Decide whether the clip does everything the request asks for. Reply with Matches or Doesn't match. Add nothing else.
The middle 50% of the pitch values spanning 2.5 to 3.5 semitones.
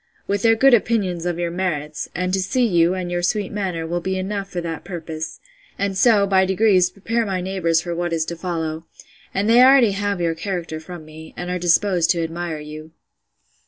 Matches